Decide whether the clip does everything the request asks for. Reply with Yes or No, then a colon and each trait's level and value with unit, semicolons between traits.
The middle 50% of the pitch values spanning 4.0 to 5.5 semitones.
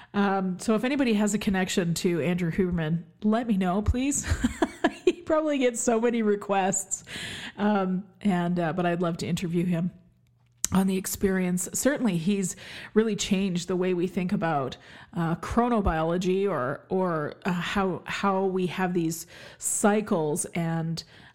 No: average, 3.3 semitones